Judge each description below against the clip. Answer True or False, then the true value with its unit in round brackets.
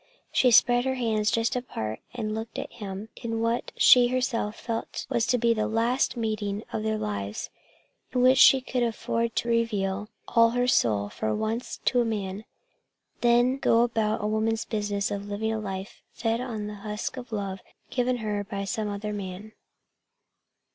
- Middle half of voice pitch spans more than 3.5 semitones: False (2.5 semitones)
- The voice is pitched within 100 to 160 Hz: False (220 Hz)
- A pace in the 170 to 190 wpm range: True (180 wpm)